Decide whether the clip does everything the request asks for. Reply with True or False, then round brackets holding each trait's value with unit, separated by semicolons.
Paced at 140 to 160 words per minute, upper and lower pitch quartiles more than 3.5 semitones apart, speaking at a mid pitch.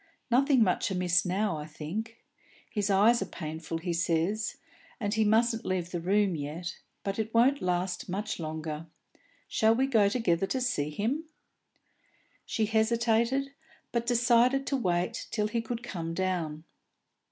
False (150 wpm; 5.1 semitones; 205 Hz)